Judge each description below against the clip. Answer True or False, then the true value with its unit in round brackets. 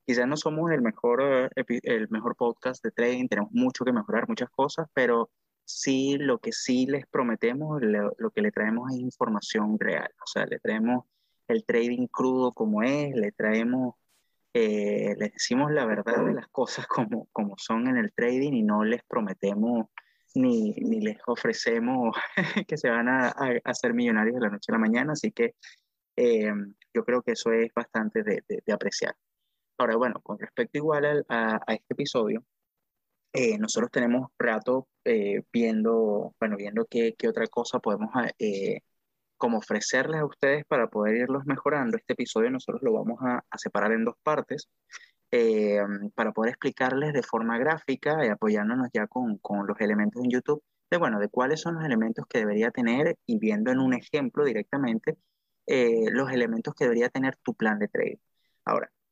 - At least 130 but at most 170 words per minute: False (180 wpm)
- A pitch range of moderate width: False (8.8 semitones)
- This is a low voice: True (130 Hz)